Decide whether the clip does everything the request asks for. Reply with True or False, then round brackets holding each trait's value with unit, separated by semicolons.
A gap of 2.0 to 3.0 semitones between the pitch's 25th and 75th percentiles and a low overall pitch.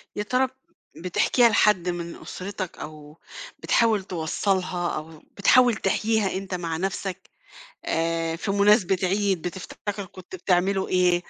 False (2.7 semitones; 185 Hz)